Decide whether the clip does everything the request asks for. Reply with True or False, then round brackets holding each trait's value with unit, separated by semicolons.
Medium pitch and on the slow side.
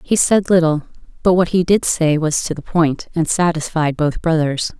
False (165 Hz; 200 wpm)